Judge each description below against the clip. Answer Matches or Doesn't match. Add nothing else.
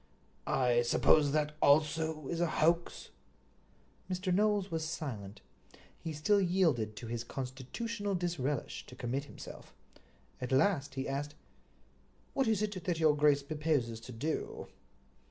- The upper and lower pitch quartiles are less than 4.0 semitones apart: Doesn't match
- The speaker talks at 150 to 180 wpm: Doesn't match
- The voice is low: Doesn't match